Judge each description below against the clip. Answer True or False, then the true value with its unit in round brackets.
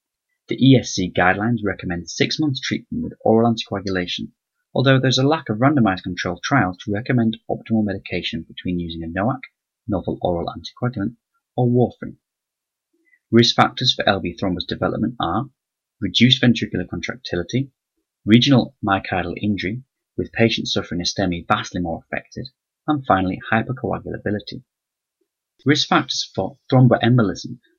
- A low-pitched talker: True (110 Hz)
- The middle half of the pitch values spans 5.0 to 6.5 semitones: True (5.3 semitones)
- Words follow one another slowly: True (125 wpm)